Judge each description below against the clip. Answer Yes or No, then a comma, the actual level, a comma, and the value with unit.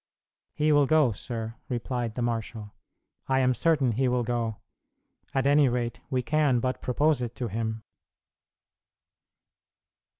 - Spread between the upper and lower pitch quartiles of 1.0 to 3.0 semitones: Yes, average, 2.7 semitones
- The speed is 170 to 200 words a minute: No, slow, 135 wpm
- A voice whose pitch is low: Yes, low, 125 Hz